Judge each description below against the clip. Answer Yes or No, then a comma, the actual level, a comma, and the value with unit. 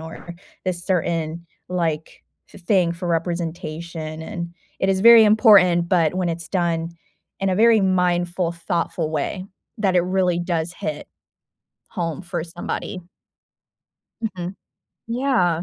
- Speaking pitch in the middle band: Yes, medium, 175 Hz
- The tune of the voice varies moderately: No, narrow, 2.0 semitones